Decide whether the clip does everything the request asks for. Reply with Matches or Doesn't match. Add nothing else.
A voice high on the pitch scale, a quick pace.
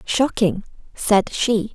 Doesn't match